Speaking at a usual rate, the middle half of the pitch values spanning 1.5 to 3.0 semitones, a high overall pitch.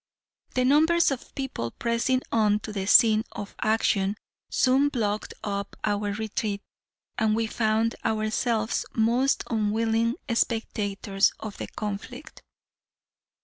No: slow, 115 wpm; narrow, 2.4 semitones; high, 220 Hz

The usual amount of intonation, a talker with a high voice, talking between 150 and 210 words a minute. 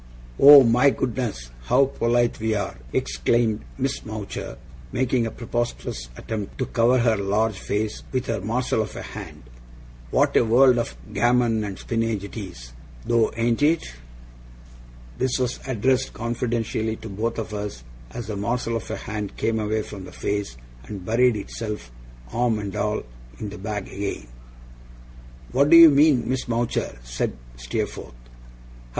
No: average, 3.1 semitones; low, 110 Hz; average, 155 wpm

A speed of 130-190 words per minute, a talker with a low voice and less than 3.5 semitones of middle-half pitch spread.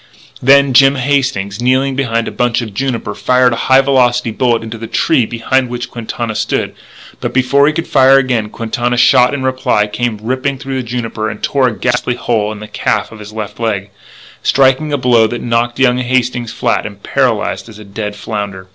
No: average, 200 wpm; low, 120 Hz; average, 3.0 semitones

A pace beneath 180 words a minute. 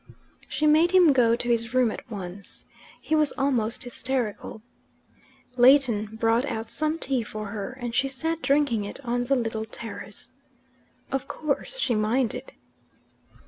Yes: average, 145 wpm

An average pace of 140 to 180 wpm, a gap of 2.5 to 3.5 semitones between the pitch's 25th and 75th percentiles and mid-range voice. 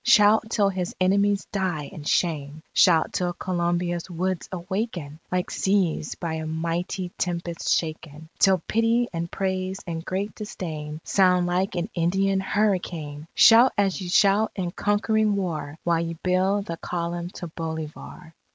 Yes: average, 145 wpm; average, 2.8 semitones; medium, 180 Hz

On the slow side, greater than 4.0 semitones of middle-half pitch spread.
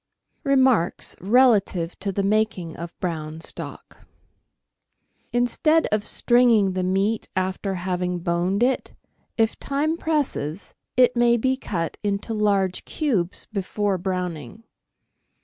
Yes: slow, 115 wpm; average, 4.9 semitones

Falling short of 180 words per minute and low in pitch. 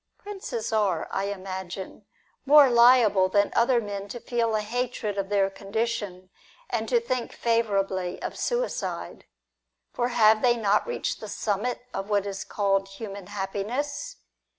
No: average, 145 wpm; high, 210 Hz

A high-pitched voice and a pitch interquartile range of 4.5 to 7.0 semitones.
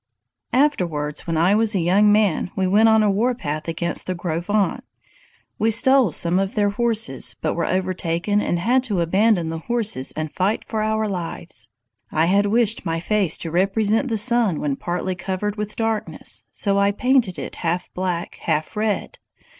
No: high, 195 Hz; average, 4.1 semitones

